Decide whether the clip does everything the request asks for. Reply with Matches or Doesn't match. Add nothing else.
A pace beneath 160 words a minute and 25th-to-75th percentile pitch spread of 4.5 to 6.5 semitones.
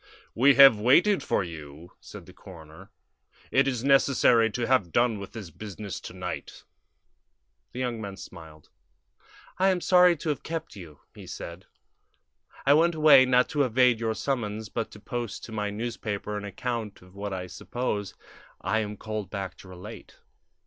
Doesn't match